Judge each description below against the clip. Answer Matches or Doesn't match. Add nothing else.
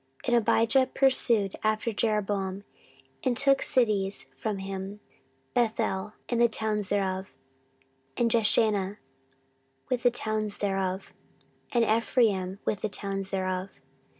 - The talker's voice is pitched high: Matches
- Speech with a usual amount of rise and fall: Matches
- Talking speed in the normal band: Doesn't match